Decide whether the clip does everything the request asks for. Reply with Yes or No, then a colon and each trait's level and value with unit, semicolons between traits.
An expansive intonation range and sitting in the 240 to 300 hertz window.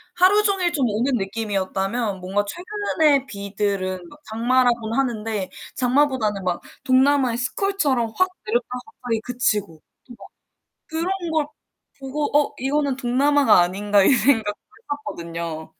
Yes: wide, 5.7 semitones; high, 245 Hz